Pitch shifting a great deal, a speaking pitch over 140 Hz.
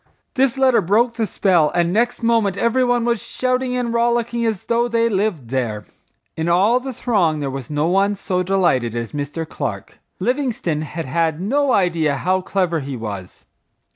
Yes: wide, 7.3 semitones; high, 190 Hz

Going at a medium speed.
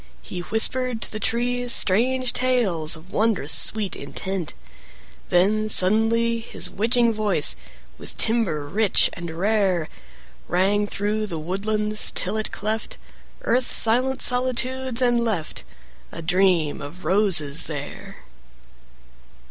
No: slow, 115 wpm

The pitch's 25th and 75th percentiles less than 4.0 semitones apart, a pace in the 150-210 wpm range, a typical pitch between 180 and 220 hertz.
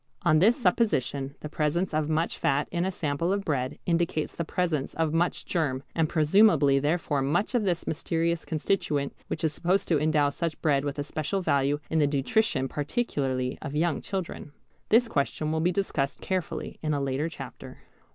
No: average, 3.4 semitones; average, 180 wpm; medium, 155 Hz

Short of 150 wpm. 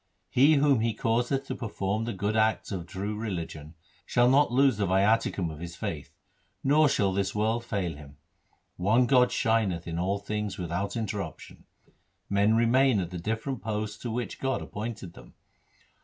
No: average, 170 wpm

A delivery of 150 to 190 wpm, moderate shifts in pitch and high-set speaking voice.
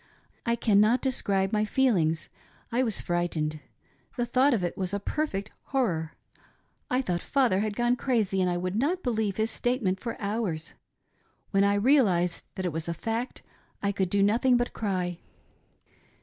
Yes: average, 170 wpm; average, 4.9 semitones; high, 205 Hz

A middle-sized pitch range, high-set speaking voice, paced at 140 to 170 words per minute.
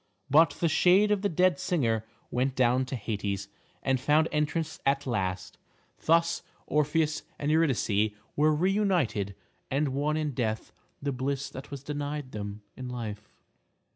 No: average, 4.8 semitones; medium, 140 Hz; average, 150 wpm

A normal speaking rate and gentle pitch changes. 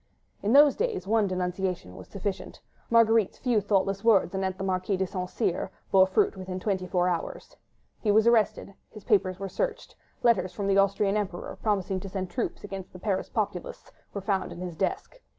Yes: average, 185 wpm; narrow, 2.3 semitones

